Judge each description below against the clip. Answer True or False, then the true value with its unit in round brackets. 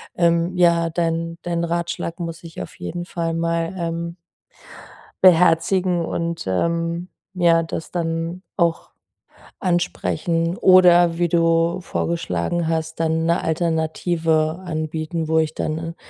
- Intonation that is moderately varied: False (0.9 semitones)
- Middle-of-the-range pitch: True (170 Hz)